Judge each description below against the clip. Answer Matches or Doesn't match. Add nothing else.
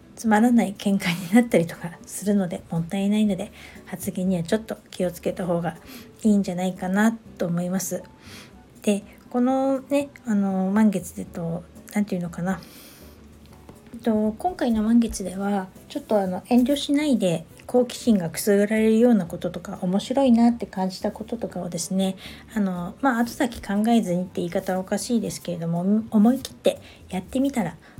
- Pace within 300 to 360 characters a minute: Matches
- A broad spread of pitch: Doesn't match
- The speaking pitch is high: Matches